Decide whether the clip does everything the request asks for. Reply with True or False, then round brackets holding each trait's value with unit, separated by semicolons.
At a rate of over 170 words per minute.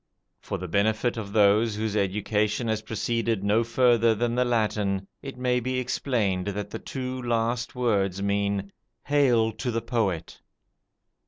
False (150 wpm)